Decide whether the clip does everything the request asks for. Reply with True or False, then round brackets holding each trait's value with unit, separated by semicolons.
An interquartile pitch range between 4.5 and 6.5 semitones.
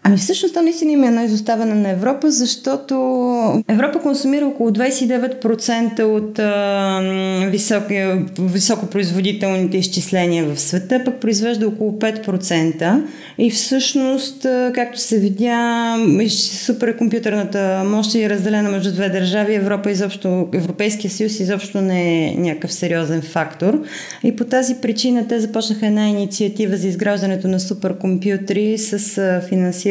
False (3.6 semitones)